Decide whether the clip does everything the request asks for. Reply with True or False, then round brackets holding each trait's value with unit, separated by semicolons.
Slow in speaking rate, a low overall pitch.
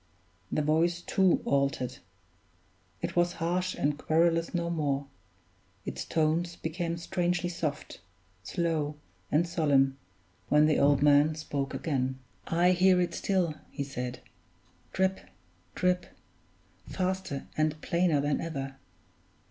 False (115 wpm; 160 Hz)